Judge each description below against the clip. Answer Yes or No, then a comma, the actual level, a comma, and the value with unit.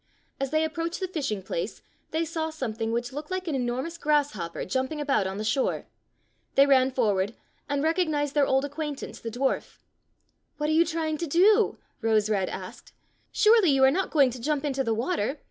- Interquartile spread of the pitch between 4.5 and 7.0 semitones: Yes, average, 4.8 semitones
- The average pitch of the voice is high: Yes, very high, 280 Hz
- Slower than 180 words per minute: No, average, 200 wpm